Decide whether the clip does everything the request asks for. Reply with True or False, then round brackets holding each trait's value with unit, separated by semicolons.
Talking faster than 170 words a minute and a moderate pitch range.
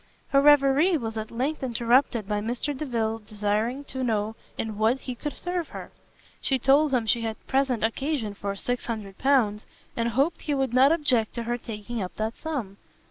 True (180 wpm; 3.9 semitones)